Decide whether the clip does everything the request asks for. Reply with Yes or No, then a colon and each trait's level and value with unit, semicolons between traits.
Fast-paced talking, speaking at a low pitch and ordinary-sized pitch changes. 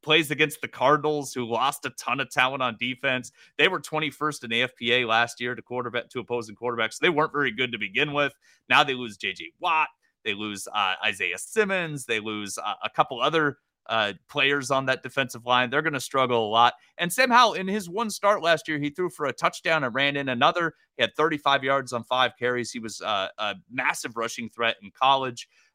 Yes: fast, 215 wpm; low, 130 Hz; average, 4.1 semitones